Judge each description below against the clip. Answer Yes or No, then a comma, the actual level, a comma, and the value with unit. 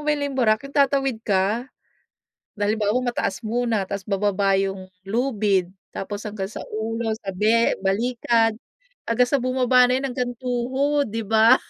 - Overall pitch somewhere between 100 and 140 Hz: No, high, 225 Hz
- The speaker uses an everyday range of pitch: Yes, average, 3.5 semitones